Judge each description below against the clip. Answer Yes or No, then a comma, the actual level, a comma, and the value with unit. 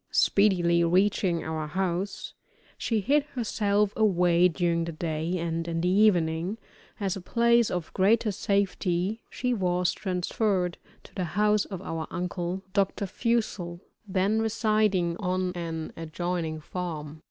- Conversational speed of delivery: No, slow, 130 wpm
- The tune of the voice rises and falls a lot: No, average, 3.2 semitones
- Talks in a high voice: No, medium, 180 Hz